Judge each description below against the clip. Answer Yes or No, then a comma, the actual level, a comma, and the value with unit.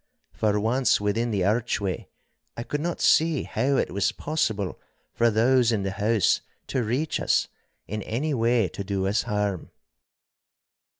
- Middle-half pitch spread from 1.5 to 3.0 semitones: No, average, 3.7 semitones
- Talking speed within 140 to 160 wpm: Yes, average, 155 wpm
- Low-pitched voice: Yes, low, 110 Hz